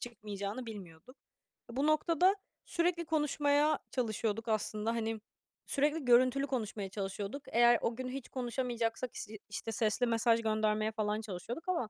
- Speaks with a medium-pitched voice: No, high, 235 Hz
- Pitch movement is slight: No, average, 4.2 semitones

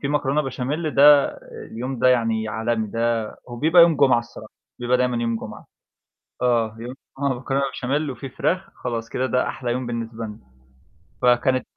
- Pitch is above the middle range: No, low, 125 Hz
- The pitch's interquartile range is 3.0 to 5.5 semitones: No, narrow, 2.6 semitones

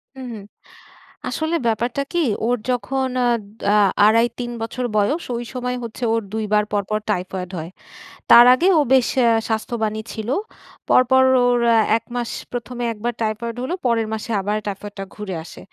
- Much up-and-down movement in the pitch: No, narrow, 2.6 semitones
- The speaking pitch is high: Yes, high, 230 Hz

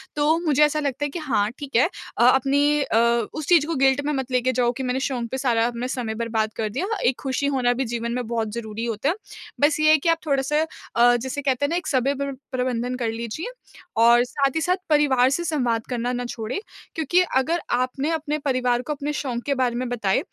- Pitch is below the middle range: No, very high, 260 Hz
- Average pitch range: Yes, average, 3.4 semitones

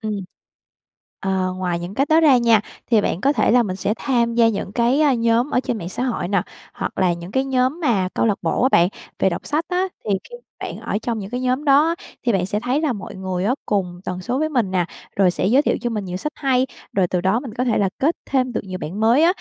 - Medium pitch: No, high, 230 Hz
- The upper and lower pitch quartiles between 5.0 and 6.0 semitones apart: Yes, wide, 5.6 semitones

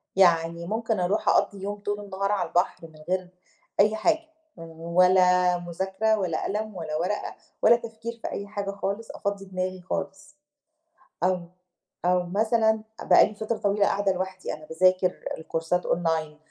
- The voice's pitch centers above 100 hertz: Yes, high, 190 Hz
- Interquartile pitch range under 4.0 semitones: Yes, average, 2.7 semitones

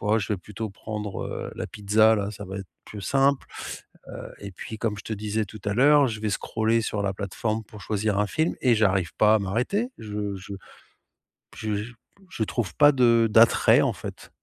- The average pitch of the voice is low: Yes, low, 110 Hz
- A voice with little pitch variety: Yes, narrow, 2.0 semitones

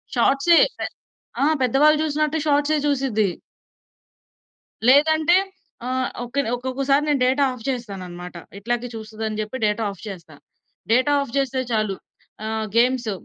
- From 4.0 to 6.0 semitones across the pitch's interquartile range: Yes, average, 4.5 semitones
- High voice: Yes, very high, 255 Hz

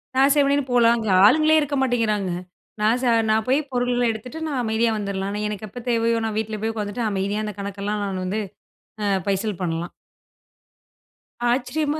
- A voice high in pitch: Yes, high, 220 Hz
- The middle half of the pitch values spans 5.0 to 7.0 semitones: No, average, 3.2 semitones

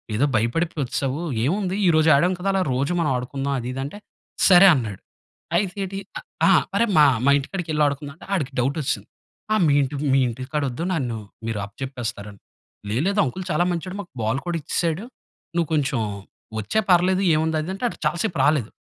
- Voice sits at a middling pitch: Yes, medium, 150 Hz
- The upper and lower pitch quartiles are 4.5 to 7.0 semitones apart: Yes, average, 5.1 semitones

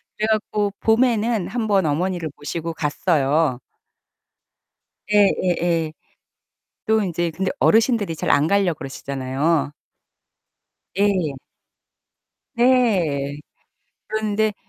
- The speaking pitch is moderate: Yes, medium, 180 Hz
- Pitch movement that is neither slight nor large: No, wide, 5.7 semitones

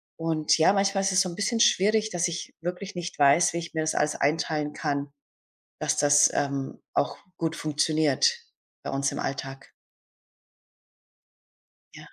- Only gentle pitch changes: No, average, 3.7 semitones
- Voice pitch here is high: No, medium, 160 Hz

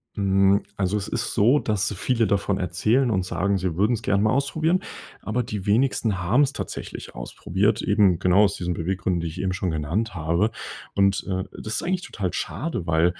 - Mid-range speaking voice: No, low, 100 Hz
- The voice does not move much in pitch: No, average, 3.3 semitones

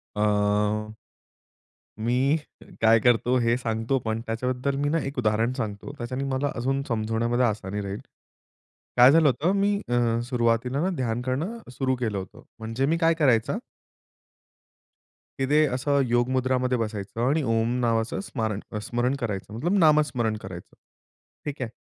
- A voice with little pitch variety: No, average, 3.3 semitones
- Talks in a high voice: No, low, 120 Hz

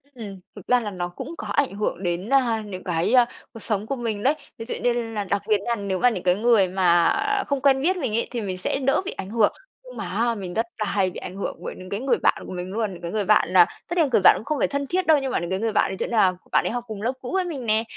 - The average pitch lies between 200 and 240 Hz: Yes, high, 220 Hz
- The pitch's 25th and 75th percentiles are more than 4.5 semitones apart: Yes, average, 5.1 semitones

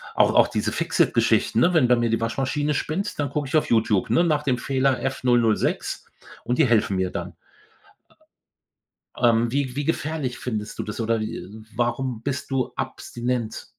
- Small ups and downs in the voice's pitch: No, average, 3.8 semitones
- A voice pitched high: No, low, 125 Hz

